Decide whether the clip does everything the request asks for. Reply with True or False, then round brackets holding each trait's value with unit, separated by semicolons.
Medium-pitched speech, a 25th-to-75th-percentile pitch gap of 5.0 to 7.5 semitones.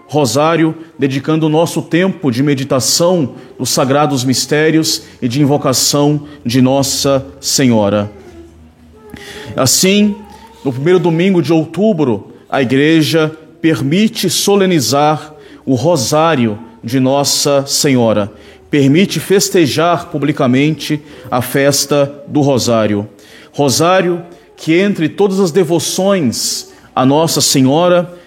False (150 Hz; 4.0 semitones)